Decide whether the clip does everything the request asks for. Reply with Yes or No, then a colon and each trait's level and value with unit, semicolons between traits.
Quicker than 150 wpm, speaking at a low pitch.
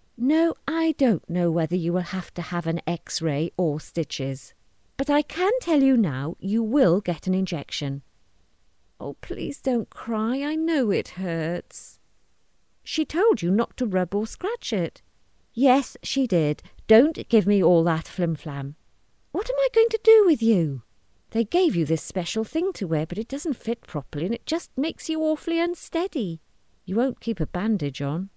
No: average, 180 wpm; high, 205 Hz